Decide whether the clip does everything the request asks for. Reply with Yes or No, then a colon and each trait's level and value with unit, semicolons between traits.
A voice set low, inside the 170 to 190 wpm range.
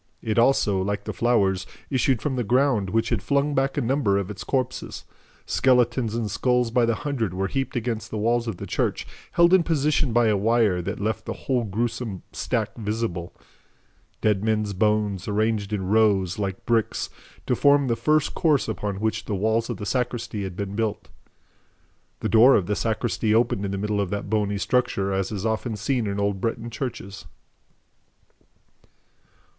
Yes: low, 110 Hz; average, 180 wpm